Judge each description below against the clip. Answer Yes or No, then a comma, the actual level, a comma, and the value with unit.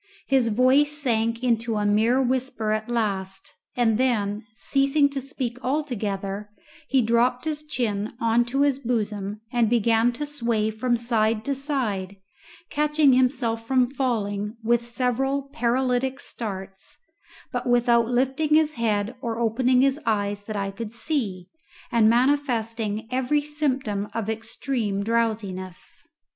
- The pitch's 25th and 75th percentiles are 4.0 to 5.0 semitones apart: No, average, 3.5 semitones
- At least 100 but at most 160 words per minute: Yes, slow, 135 wpm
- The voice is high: Yes, high, 235 Hz